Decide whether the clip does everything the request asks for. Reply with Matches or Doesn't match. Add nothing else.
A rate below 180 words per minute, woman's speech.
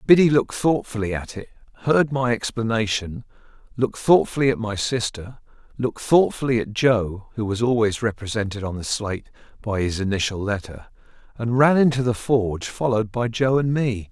Doesn't match